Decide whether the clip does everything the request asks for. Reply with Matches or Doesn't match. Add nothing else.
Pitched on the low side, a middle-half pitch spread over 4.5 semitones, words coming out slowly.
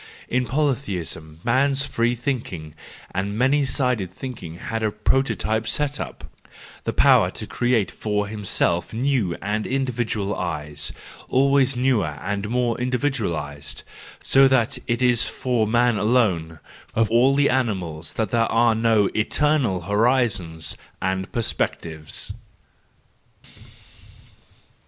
Matches